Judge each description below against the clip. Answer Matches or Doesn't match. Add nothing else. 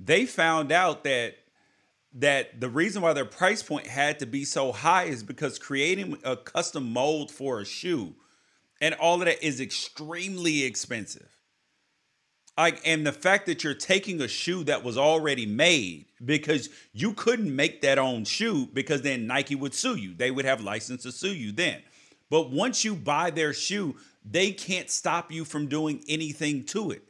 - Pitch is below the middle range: Doesn't match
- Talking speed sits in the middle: Matches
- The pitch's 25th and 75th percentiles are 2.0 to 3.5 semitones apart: Doesn't match